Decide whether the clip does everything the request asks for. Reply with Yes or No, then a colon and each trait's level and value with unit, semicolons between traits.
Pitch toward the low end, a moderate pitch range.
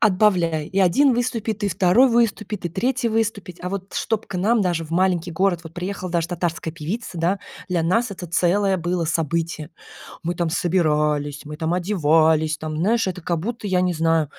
No: medium, 180 Hz; average, 3.7 semitones